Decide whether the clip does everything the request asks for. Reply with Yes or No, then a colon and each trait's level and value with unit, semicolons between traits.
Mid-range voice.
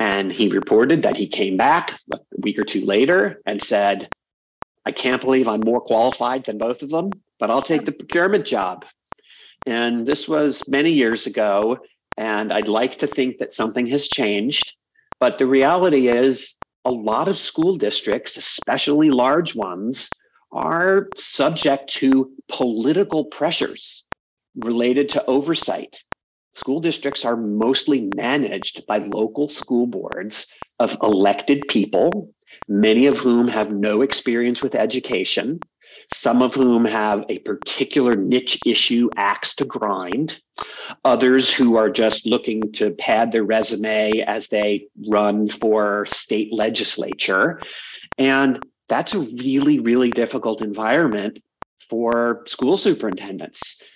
No: low, 125 Hz